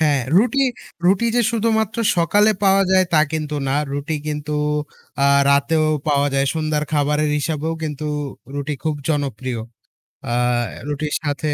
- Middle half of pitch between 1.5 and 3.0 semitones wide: No, average, 3.5 semitones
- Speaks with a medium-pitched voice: Yes, medium, 155 Hz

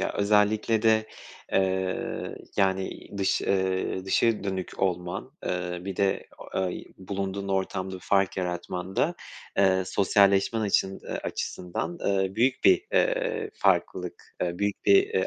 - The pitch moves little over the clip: Yes, narrow, 2.0 semitones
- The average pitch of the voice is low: Yes, very low, 95 Hz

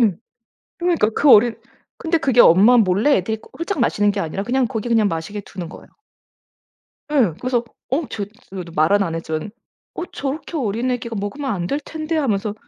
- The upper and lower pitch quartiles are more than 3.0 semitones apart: Yes, wide, 5.5 semitones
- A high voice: Yes, high, 225 Hz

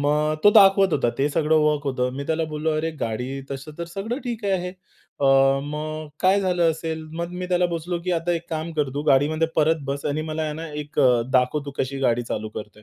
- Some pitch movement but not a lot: Yes, average, 3.2 semitones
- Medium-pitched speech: Yes, medium, 155 Hz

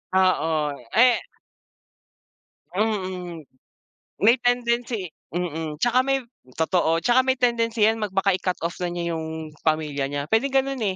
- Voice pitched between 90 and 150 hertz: No, high, 190 Hz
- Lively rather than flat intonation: Yes, wide, 6.5 semitones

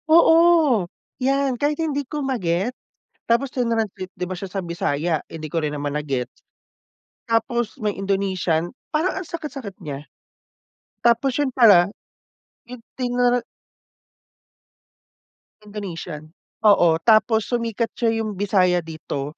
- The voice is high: Yes, high, 215 Hz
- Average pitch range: No, wide, 6.3 semitones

